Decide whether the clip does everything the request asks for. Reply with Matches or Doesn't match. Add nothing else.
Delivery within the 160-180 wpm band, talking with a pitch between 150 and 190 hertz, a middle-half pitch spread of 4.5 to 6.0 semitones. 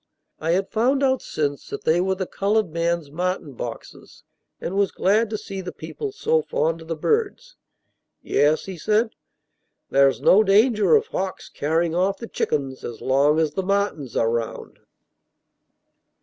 Matches